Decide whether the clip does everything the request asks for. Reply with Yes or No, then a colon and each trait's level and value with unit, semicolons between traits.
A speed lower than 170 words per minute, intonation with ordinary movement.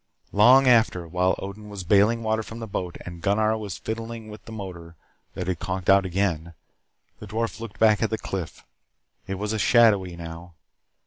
No: average, 180 wpm; average, 3.5 semitones